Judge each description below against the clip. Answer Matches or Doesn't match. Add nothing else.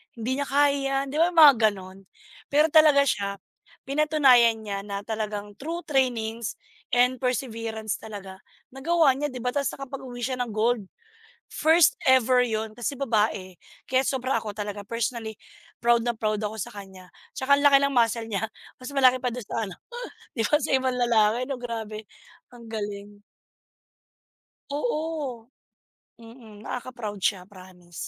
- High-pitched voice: Matches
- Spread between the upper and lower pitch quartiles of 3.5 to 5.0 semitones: Matches